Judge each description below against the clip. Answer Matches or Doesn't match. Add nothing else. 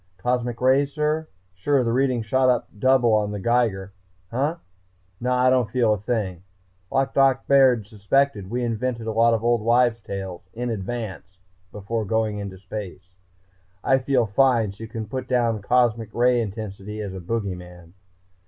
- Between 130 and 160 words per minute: Doesn't match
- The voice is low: Matches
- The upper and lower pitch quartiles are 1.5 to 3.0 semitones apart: Doesn't match